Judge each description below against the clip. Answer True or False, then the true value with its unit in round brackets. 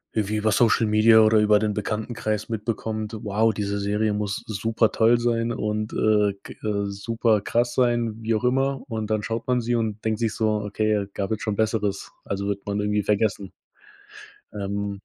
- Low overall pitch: True (110 Hz)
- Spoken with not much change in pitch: True (1.6 semitones)